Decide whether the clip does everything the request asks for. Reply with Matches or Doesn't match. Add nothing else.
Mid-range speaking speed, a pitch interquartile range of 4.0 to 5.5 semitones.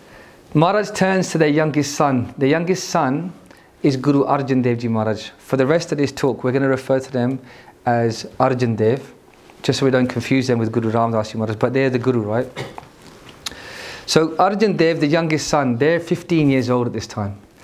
Matches